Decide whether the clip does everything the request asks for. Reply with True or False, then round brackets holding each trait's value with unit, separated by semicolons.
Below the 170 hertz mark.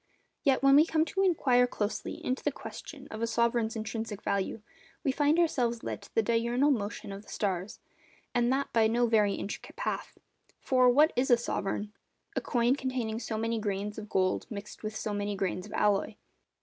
False (230 Hz)